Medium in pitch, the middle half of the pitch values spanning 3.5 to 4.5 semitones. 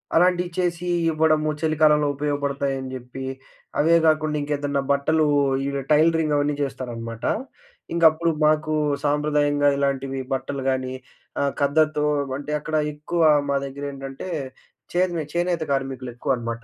No: medium, 145 Hz; narrow, 2.4 semitones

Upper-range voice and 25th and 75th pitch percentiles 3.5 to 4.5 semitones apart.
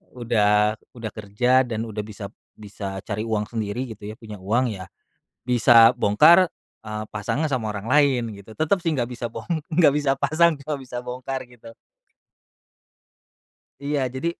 No: low, 115 Hz; average, 4.0 semitones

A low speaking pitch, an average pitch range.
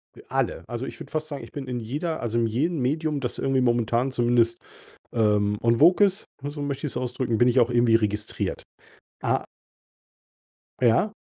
Yes: low, 125 Hz; average, 3.7 semitones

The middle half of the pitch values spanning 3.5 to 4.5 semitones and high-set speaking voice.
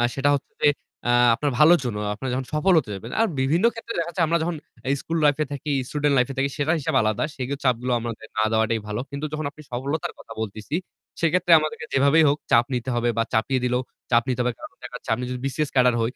No: average, 4.1 semitones; low, 135 Hz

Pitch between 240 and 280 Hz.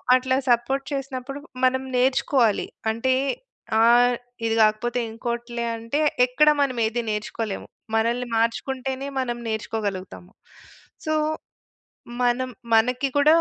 Yes: high, 245 Hz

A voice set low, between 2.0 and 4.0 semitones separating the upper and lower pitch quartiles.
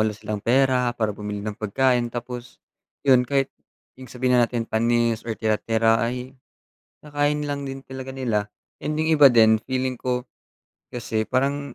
Yes: low, 125 Hz; average, 2.9 semitones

